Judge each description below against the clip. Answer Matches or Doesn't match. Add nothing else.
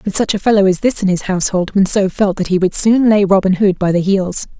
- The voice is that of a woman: Matches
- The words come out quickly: Matches